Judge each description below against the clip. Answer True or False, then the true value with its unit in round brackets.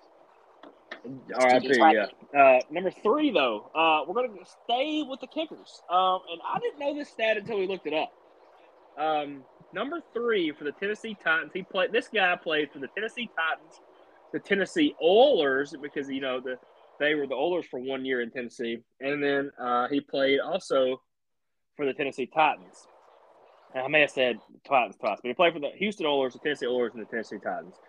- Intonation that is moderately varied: False (8.7 semitones)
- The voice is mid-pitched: True (160 Hz)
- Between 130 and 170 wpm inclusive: False (190 wpm)